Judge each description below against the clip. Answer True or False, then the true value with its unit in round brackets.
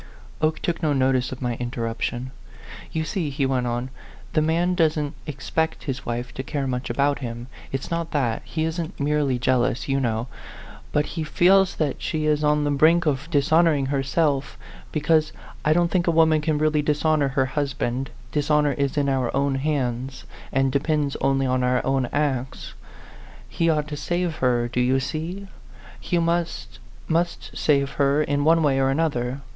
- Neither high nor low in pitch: True (145 Hz)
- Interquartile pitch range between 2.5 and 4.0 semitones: True (3.1 semitones)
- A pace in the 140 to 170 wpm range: False (180 wpm)